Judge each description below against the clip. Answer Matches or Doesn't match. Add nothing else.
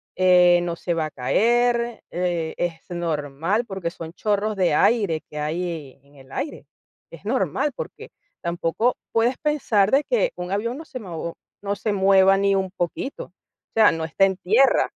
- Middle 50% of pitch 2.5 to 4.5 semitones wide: Doesn't match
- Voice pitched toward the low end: Doesn't match